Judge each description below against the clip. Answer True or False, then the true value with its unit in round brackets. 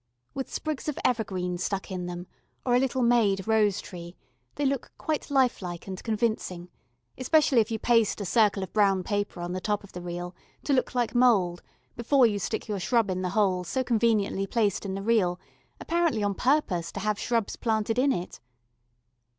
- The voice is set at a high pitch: True (210 Hz)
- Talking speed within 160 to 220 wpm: True (190 wpm)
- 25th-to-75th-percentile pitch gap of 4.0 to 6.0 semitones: True (4.6 semitones)